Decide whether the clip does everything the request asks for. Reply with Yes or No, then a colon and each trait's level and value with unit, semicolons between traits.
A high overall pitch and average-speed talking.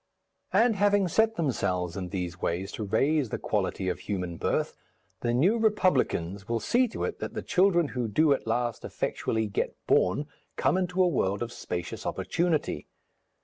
No: low, 120 Hz; average, 170 wpm